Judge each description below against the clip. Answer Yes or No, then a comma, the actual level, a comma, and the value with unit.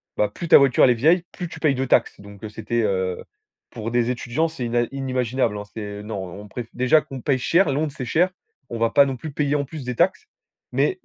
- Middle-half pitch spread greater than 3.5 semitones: Yes, average, 4.5 semitones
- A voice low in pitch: Yes, low, 125 Hz